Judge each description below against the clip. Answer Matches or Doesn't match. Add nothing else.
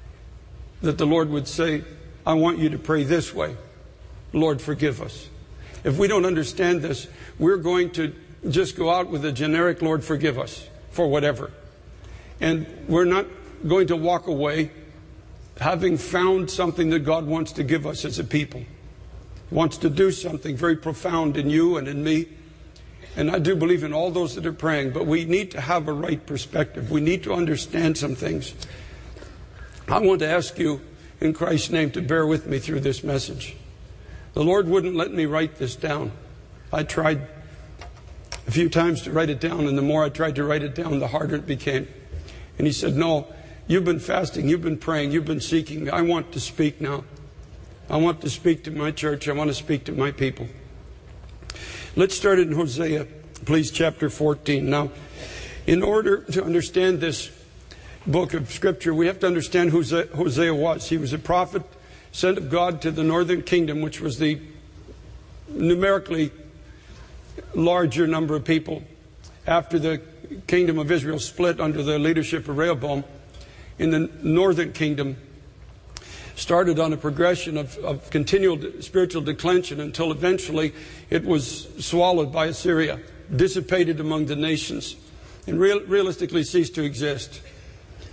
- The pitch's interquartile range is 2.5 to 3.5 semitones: Matches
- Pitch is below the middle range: Doesn't match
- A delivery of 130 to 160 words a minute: Doesn't match